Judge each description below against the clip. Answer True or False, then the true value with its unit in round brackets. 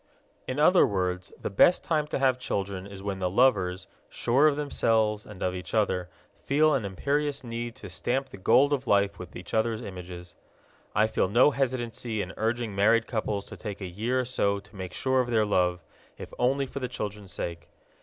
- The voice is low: True (110 Hz)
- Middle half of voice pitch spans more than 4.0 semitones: True (5.1 semitones)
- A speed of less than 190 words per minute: False (200 wpm)